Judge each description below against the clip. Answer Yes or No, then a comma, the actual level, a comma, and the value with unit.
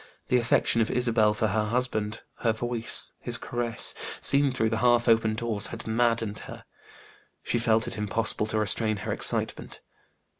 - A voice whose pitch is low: Yes, low, 115 Hz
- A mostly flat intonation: Yes, narrow, 1.6 semitones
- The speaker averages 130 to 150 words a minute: No, average, 160 wpm